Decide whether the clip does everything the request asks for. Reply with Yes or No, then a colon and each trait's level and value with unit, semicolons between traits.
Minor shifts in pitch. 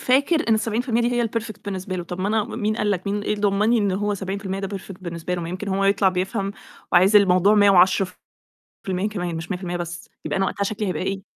Yes: narrow, 2.3 semitones